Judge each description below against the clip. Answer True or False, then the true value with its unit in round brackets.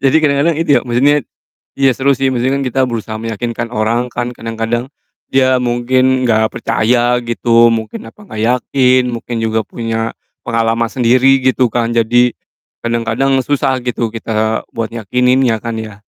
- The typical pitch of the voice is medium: False (120 Hz)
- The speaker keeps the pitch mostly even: True (2.2 semitones)